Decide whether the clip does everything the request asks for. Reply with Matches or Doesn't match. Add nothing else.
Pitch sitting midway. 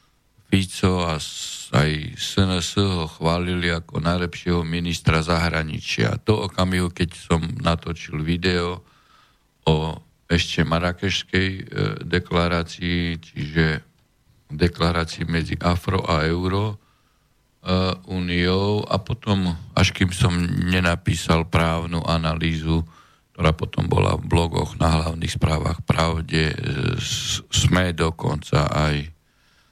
Doesn't match